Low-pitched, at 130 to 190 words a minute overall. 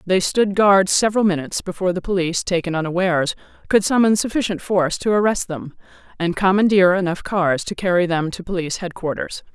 No: medium, 185 Hz; average, 170 wpm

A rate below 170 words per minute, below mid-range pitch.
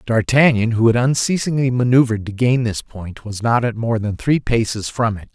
No: average, 200 wpm; low, 115 Hz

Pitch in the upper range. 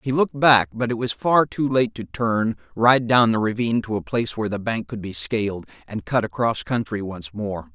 No: low, 110 Hz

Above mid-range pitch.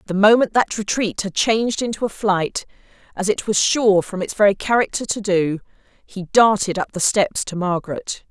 Yes: high, 205 Hz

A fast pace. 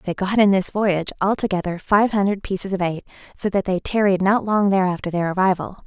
Yes: fast, 225 wpm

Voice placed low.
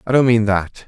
Yes: low, 110 Hz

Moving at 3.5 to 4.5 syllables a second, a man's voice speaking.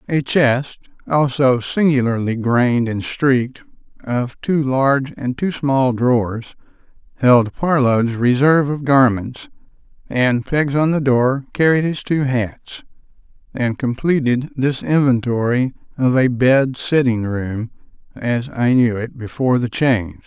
Yes: 4.0 syllables/s; male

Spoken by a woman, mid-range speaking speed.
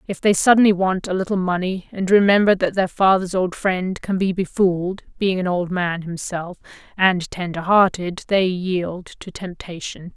Yes: female; average, 170 wpm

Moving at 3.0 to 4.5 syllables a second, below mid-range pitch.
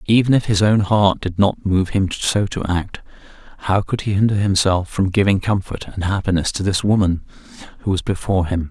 No: 5.4 syllables/s; very low, 95 Hz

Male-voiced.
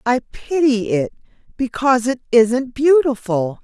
No: female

